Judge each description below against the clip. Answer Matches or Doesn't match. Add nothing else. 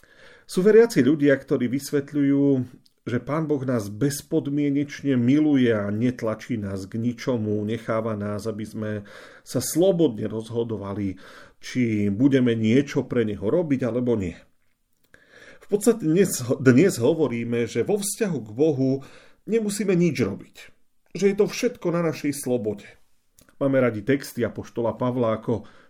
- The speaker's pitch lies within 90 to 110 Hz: Doesn't match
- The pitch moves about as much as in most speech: Matches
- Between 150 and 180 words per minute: Doesn't match